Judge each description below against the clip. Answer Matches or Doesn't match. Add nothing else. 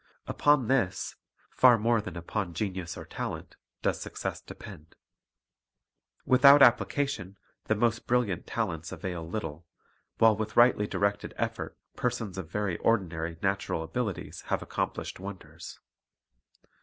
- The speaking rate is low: Matches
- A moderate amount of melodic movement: Matches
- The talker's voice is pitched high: Doesn't match